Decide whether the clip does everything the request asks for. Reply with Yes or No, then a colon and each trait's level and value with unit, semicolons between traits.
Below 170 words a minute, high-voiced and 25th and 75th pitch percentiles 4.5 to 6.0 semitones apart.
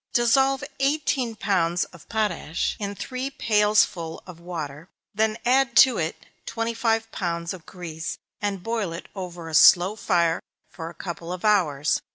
Yes: average, 160 wpm; high, 195 Hz; average, 5.1 semitones